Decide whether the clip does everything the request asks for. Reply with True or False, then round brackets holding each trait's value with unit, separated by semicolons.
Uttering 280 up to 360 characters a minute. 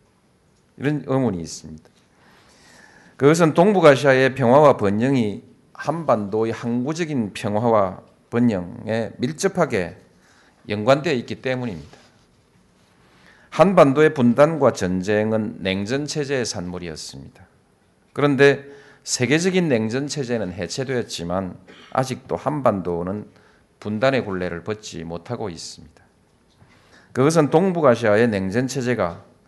False (265 characters per minute)